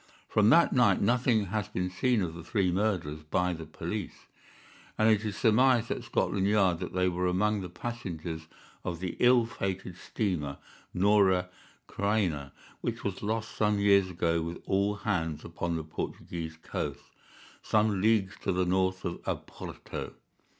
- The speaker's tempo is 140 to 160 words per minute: Yes, average, 155 wpm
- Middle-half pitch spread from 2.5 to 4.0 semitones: Yes, average, 3.5 semitones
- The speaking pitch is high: No, very low, 95 Hz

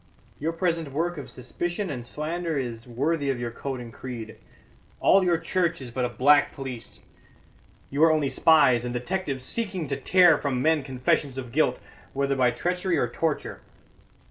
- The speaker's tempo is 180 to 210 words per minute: No, average, 170 wpm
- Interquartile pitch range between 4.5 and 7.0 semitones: Yes, average, 4.8 semitones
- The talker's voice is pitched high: No, medium, 140 Hz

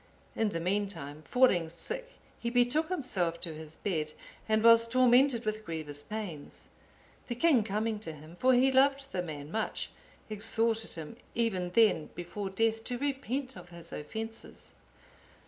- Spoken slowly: No, average, 150 wpm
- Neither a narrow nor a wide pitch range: No, wide, 6.2 semitones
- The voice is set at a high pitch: Yes, high, 215 Hz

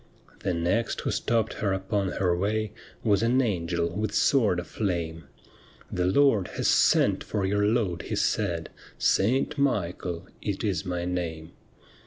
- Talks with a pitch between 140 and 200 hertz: No, very low, 95 Hz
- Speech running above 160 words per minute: No, average, 155 wpm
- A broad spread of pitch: No, average, 3.7 semitones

